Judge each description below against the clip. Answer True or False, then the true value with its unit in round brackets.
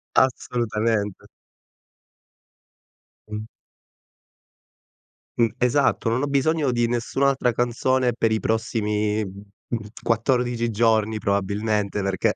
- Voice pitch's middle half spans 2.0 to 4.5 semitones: True (2.5 semitones)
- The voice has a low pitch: True (115 Hz)